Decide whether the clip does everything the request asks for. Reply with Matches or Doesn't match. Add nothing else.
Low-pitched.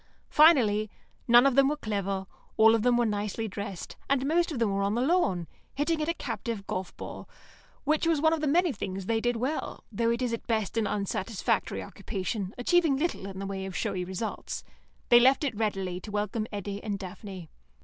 Doesn't match